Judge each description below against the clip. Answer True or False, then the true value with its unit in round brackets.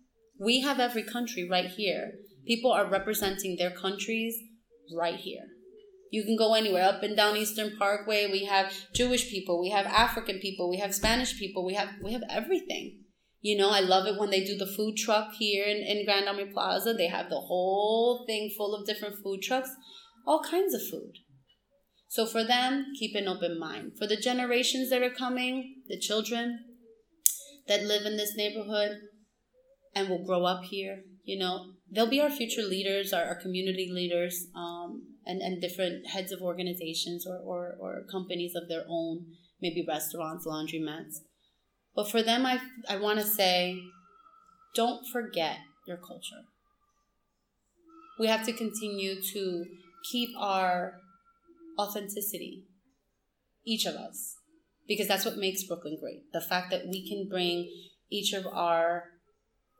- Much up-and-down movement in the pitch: False (4.1 semitones)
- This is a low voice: False (205 Hz)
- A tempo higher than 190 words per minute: False (160 wpm)